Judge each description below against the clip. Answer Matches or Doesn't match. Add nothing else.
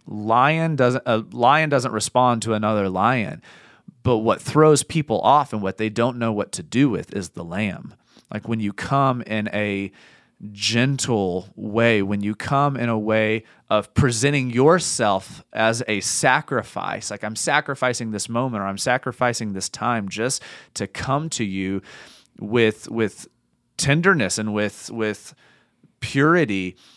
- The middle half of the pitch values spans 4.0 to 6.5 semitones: Doesn't match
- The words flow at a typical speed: Matches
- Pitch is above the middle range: Doesn't match